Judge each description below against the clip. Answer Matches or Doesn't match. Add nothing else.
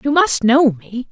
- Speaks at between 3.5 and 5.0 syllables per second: Matches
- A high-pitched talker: Matches